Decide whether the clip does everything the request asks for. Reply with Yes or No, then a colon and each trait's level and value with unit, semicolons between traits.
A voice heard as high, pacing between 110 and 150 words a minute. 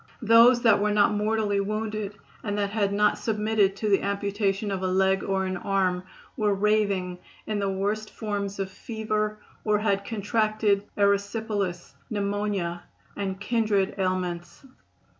Yes: high, 205 Hz; average, 140 wpm